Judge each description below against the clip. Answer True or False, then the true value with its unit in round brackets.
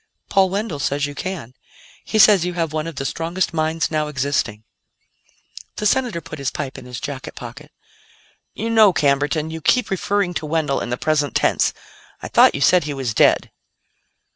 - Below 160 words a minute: False (185 wpm)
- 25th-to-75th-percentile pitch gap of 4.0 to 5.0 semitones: True (4.3 semitones)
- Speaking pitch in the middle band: True (155 Hz)